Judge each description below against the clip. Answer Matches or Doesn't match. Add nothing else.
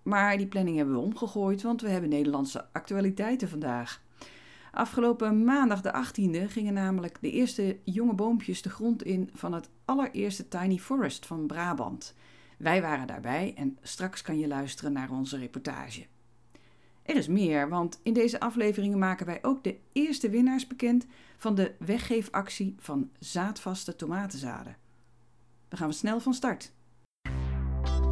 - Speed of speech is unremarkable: Matches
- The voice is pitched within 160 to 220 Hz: Matches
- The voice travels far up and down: Matches